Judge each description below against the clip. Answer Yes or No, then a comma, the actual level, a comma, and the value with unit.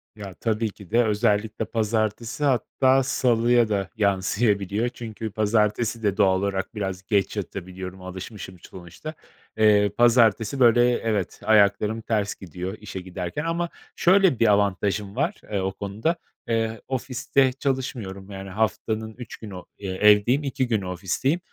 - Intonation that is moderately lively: Yes, average, 3.4 semitones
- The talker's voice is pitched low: Yes, low, 110 Hz